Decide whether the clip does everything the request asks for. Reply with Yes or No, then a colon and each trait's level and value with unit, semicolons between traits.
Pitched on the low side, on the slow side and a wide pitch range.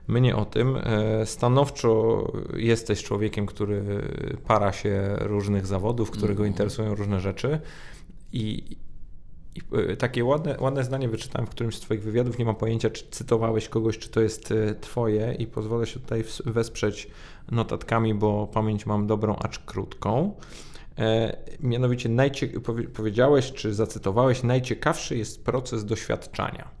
No: low, 110 Hz; slow, 130 wpm; narrow, 2.6 semitones